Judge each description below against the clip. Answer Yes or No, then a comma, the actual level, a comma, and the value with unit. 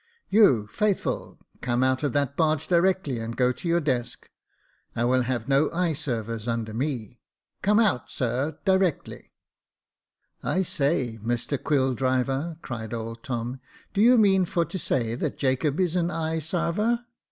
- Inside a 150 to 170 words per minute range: Yes, average, 165 wpm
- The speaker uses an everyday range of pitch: No, wide, 6.0 semitones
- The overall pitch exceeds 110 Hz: Yes, medium, 140 Hz